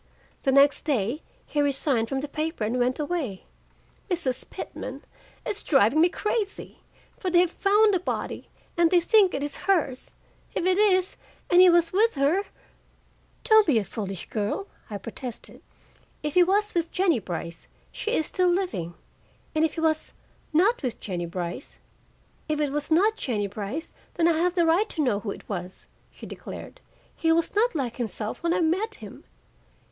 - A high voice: Yes, very high, 315 Hz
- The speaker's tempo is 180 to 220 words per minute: Yes, average, 185 wpm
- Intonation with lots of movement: Yes, wide, 6.9 semitones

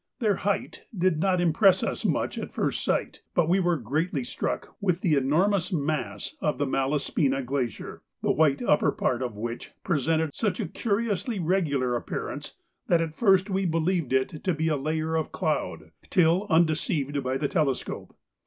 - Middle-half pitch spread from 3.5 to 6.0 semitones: Yes, average, 4.7 semitones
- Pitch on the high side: No, medium, 160 Hz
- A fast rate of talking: No, average, 170 wpm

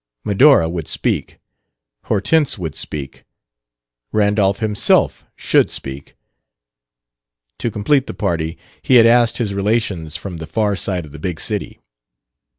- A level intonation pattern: No, wide, 5.4 semitones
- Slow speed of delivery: Yes, slow, 130 wpm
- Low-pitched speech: Yes, low, 100 Hz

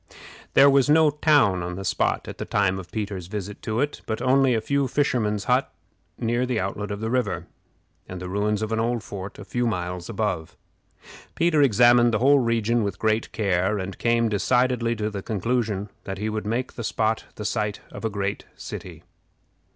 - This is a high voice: No, low, 110 Hz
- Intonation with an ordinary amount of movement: Yes, average, 3.3 semitones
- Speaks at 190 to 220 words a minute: Yes, average, 195 wpm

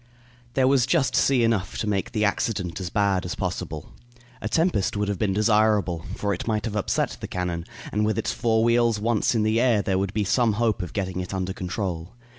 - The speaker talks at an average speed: No, fast, 220 wpm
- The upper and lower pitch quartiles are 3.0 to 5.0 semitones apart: Yes, average, 3.4 semitones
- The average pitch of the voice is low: Yes, low, 105 Hz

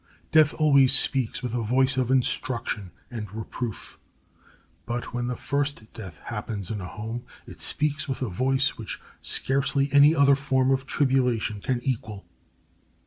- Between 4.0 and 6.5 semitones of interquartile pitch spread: No, average, 3.5 semitones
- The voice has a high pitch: No, low, 130 Hz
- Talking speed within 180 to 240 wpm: No, average, 150 wpm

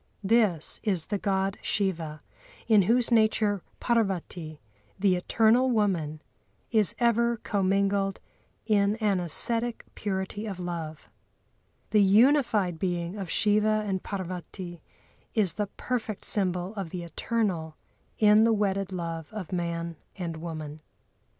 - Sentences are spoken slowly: Yes, slow, 120 wpm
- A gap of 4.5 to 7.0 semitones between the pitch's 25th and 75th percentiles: No, average, 3.7 semitones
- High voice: Yes, high, 195 Hz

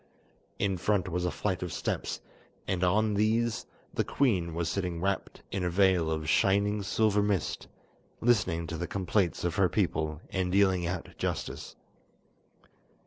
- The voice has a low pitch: Yes, very low, 95 Hz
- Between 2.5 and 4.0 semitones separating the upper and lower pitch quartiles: Yes, average, 2.9 semitones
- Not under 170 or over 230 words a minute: No, average, 150 wpm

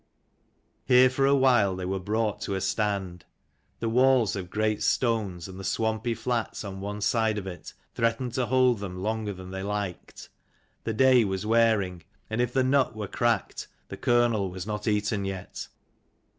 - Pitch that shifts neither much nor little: Yes, average, 3.6 semitones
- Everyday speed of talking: Yes, average, 175 wpm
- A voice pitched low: Yes, low, 110 Hz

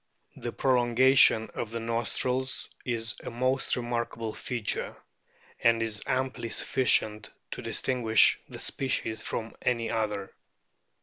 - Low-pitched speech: Yes, low, 115 Hz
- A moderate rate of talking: No, slow, 115 wpm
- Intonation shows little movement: Yes, narrow, 2.2 semitones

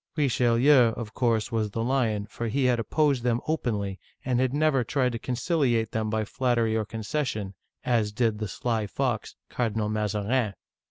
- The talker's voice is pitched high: No, low, 115 Hz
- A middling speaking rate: Yes, average, 170 wpm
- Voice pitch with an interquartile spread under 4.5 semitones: Yes, average, 2.9 semitones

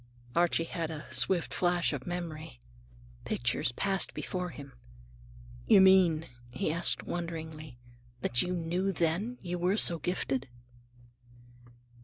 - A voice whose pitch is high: No, medium, 170 Hz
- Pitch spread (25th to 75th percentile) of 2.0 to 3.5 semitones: Yes, narrow, 2.5 semitones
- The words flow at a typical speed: No, slow, 125 wpm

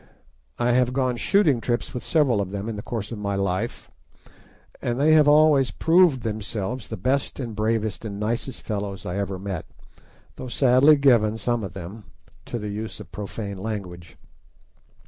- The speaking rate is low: No, average, 170 wpm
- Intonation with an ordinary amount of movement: Yes, average, 4.2 semitones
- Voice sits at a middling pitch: No, low, 110 Hz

